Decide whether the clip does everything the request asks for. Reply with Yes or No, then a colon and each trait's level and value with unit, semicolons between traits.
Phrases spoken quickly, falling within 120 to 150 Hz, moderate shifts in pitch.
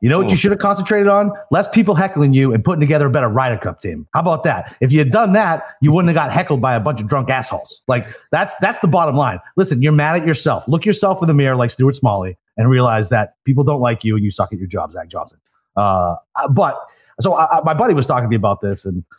No: fast, 270 wpm; low, 135 Hz; wide, 6.5 semitones